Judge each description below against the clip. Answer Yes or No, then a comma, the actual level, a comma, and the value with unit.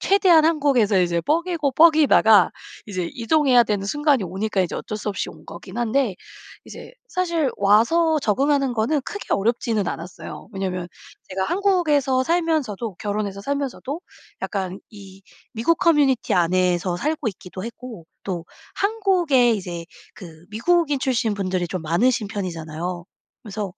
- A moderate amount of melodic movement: No, wide, 7.7 semitones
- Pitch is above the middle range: Yes, high, 225 Hz